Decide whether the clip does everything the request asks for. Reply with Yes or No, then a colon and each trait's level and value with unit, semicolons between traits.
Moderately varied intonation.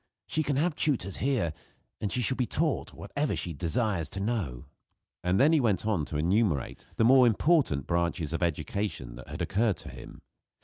No: wide, 7.5 semitones